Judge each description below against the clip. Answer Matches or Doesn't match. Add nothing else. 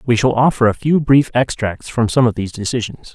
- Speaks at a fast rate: Matches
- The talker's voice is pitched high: Doesn't match